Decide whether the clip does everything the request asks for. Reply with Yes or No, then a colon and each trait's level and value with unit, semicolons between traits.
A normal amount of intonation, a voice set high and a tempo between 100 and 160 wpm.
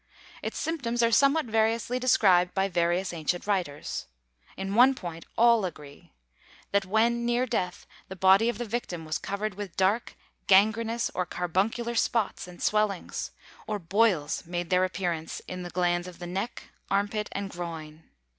Yes: average, 4.4 semitones; high, 195 Hz; average, 155 wpm